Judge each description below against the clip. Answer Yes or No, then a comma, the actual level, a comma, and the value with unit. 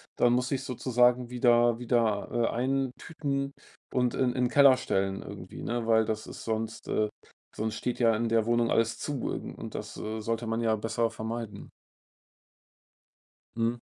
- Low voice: Yes, low, 120 Hz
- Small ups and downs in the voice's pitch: Yes, narrow, 1.8 semitones